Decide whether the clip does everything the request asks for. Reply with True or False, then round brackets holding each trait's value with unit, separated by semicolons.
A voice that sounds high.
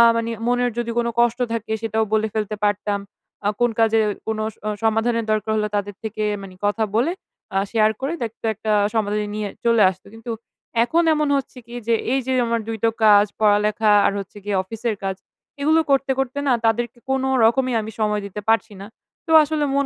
True (225 Hz)